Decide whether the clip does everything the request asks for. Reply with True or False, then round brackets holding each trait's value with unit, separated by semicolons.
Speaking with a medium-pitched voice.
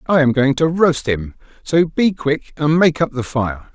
True (145 Hz)